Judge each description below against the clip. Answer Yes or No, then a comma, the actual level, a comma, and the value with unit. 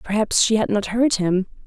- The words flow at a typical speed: No, fast, 215 wpm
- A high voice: Yes, high, 210 Hz